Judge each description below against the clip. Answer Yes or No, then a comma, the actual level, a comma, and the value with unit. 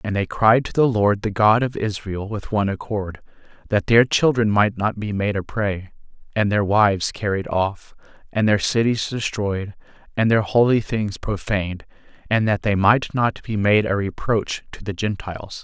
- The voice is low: Yes, low, 105 Hz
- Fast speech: No, average, 185 wpm